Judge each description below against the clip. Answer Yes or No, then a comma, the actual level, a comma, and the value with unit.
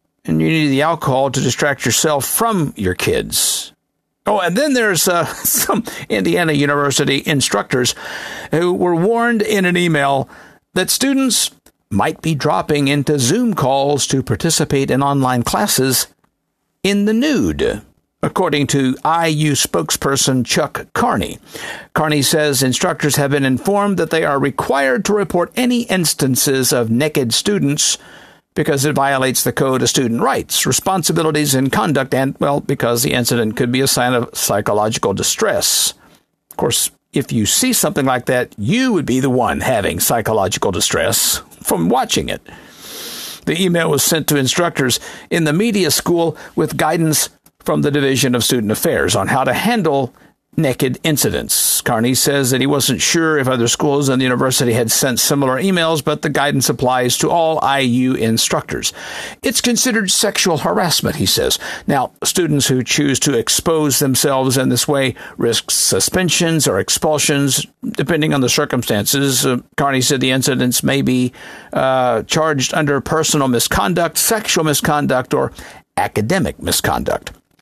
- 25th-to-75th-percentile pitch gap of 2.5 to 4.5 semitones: Yes, average, 3.9 semitones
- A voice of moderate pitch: Yes, medium, 145 Hz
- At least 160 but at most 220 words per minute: No, average, 150 wpm